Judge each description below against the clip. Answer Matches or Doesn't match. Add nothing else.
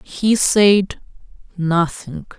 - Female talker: Matches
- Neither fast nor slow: Doesn't match